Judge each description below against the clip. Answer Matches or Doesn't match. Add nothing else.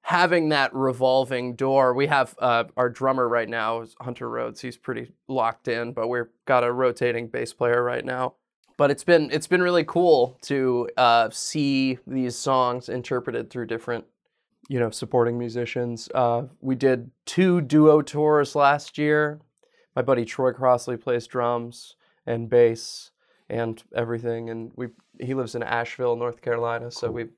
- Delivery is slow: Doesn't match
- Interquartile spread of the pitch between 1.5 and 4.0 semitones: Matches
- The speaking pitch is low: Matches